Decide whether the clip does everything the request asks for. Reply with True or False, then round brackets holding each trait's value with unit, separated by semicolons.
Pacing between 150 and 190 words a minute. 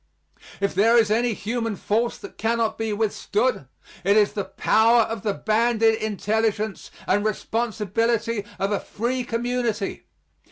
False (135 wpm)